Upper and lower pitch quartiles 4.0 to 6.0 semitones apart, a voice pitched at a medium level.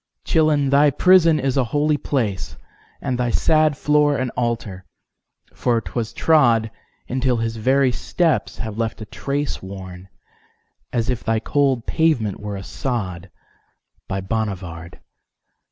No: wide, 5.4 semitones; low, 120 Hz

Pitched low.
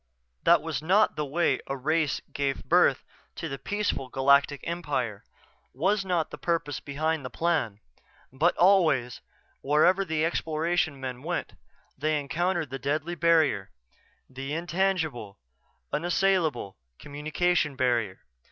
No: medium, 155 Hz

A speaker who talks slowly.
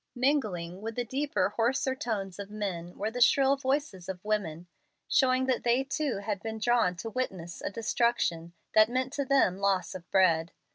No: average, 180 wpm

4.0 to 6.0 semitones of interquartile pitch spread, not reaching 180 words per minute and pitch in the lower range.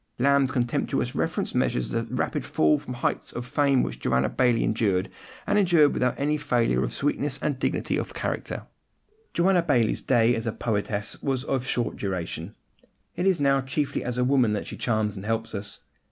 No: average, 4.4 semitones; average, 185 wpm; low, 125 Hz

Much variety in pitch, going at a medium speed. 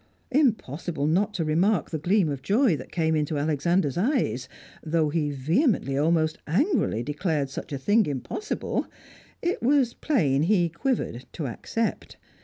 Yes: wide, 6.6 semitones; average, 145 wpm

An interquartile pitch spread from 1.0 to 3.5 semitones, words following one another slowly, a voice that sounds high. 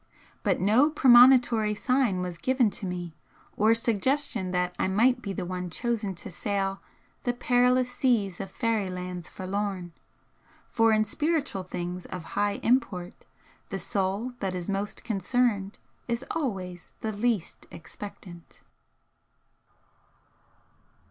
No: average, 4.8 semitones; slow, 125 wpm; high, 205 Hz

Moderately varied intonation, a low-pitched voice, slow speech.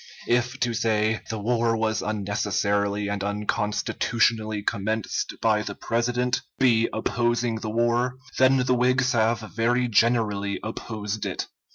No: narrow, 2.3 semitones; low, 115 Hz; slow, 130 wpm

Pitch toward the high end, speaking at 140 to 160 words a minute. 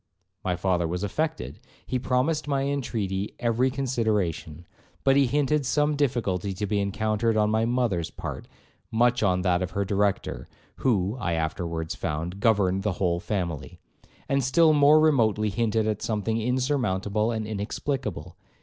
No: low, 110 Hz; average, 150 wpm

